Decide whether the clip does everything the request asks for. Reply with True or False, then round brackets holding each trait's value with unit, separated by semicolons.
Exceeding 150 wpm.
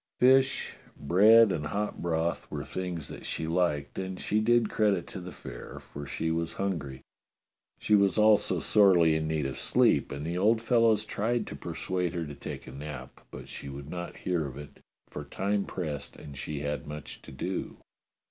True (185 wpm)